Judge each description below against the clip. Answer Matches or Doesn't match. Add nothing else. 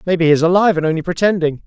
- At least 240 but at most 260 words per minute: Matches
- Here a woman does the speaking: Doesn't match